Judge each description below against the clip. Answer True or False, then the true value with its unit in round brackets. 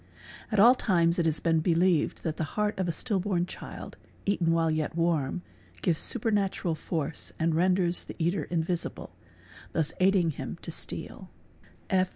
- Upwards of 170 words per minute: False (150 wpm)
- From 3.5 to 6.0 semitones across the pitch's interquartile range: False (2.6 semitones)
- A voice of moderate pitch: True (170 Hz)